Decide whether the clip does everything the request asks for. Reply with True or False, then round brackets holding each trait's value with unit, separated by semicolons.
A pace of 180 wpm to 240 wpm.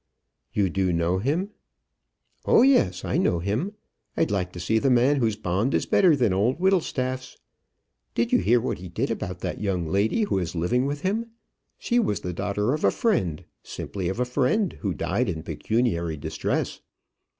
True (185 wpm)